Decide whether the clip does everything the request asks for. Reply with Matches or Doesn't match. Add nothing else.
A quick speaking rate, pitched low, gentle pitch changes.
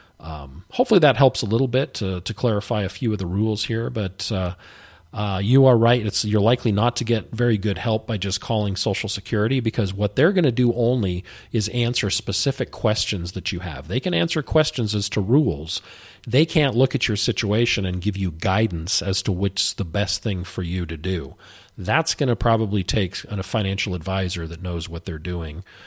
Doesn't match